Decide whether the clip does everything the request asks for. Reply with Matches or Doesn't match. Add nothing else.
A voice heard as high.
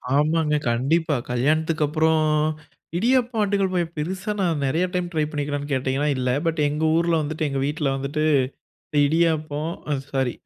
Doesn't match